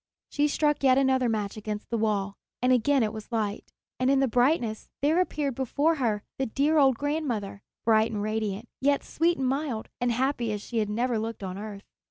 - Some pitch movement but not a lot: Yes, average, 4.3 semitones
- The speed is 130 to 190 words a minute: No, fast, 205 wpm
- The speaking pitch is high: Yes, high, 240 Hz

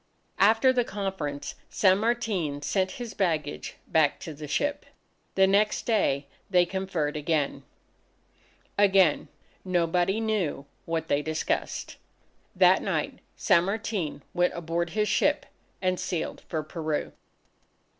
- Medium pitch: Yes, medium, 180 Hz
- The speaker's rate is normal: No, slow, 120 wpm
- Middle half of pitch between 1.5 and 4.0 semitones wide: No, average, 4.4 semitones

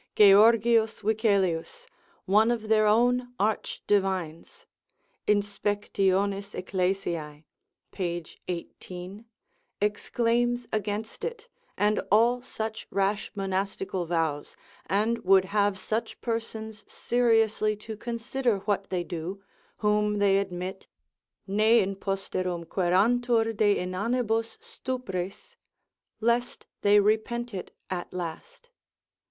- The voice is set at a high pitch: Yes, high, 205 Hz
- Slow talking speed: Yes, slow, 100 wpm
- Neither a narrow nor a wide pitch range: Yes, average, 3.0 semitones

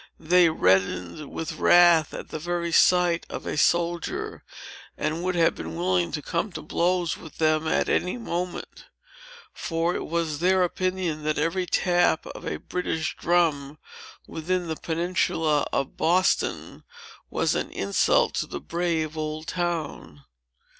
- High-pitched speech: No, medium, 170 Hz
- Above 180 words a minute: No, average, 145 wpm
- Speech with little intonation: Yes, narrow, 2.2 semitones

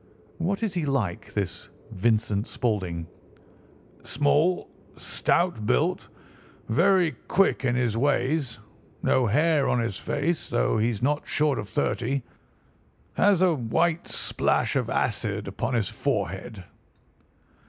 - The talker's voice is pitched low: Yes, low, 130 Hz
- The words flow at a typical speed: No, slow, 120 wpm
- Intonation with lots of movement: Yes, wide, 6.6 semitones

